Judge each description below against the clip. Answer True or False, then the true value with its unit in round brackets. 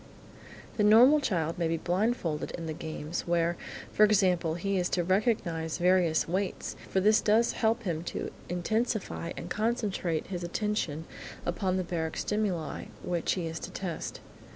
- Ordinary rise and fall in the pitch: True (4.0 semitones)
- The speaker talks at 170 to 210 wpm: False (155 wpm)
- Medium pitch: True (180 Hz)